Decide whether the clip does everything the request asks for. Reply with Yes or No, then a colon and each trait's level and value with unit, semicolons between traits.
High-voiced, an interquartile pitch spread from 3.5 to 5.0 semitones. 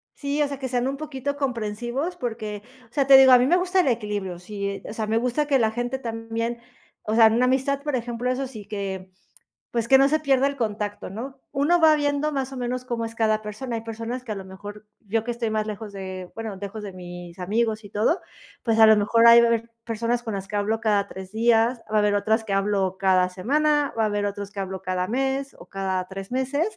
Yes: high, 225 Hz; average, 4.2 semitones